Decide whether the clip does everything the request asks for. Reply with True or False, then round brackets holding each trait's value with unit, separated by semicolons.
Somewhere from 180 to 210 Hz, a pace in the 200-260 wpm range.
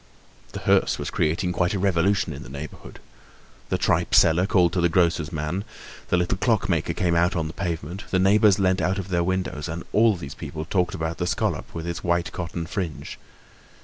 False (85 Hz; 205 wpm)